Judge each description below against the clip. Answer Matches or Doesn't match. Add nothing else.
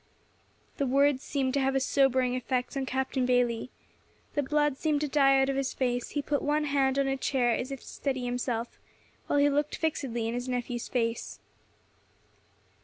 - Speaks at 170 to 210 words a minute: Matches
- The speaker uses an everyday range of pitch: Doesn't match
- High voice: Matches